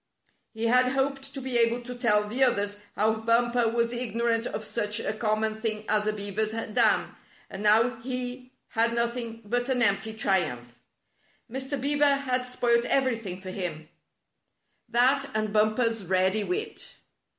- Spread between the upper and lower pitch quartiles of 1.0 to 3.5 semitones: Yes, average, 2.8 semitones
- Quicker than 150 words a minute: Yes, average, 160 wpm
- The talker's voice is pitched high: Yes, high, 230 Hz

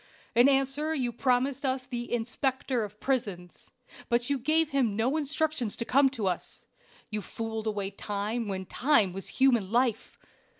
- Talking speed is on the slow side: No, average, 160 wpm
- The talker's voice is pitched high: Yes, high, 240 Hz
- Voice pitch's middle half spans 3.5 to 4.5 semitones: Yes, average, 4.2 semitones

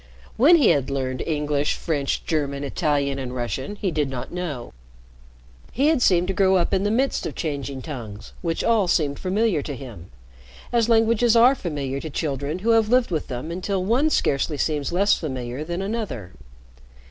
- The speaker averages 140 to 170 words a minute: No, average, 180 wpm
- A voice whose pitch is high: No, medium, 160 Hz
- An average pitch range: No, wide, 6.9 semitones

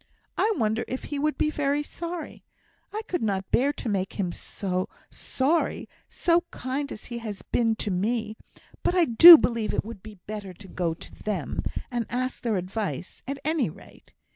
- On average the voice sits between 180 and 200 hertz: No, high, 230 Hz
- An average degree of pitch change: No, wide, 6.1 semitones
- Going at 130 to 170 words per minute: No, average, 180 wpm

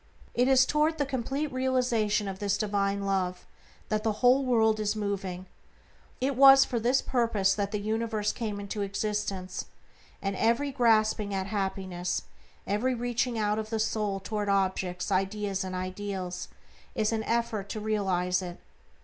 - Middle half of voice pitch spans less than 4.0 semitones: Yes, average, 3.2 semitones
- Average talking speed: Yes, average, 155 wpm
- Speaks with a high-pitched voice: Yes, high, 210 Hz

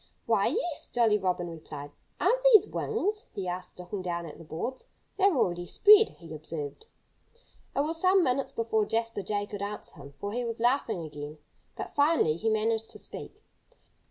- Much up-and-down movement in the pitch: Yes, wide, 7.8 semitones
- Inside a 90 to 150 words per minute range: No, average, 175 wpm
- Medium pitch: No, high, 210 Hz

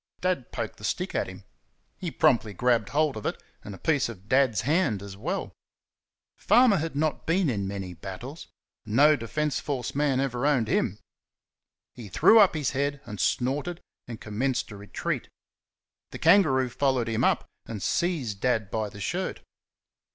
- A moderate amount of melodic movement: No, wide, 5.8 semitones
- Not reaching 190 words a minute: Yes, average, 165 wpm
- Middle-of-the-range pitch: No, low, 125 Hz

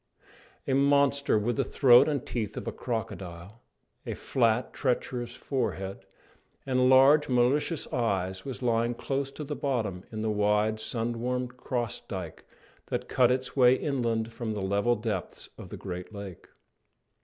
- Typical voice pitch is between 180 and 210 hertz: No, low, 120 Hz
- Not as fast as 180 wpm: Yes, average, 155 wpm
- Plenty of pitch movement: No, average, 3.7 semitones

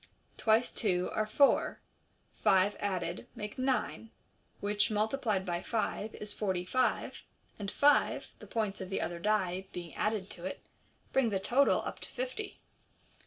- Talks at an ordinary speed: Yes, average, 150 wpm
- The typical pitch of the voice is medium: No, high, 210 Hz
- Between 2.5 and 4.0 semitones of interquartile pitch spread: Yes, average, 3.2 semitones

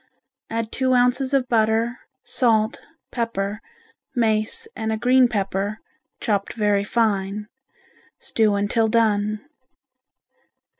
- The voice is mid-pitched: No, high, 220 Hz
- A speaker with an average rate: No, slow, 100 wpm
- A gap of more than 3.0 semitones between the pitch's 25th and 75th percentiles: No, narrow, 2.4 semitones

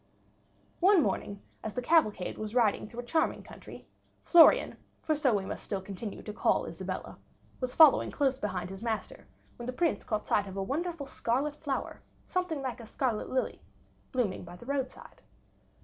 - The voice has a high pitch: Yes, high, 245 Hz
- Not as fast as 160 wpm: No, average, 175 wpm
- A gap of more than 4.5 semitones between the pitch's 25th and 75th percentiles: Yes, wide, 5.5 semitones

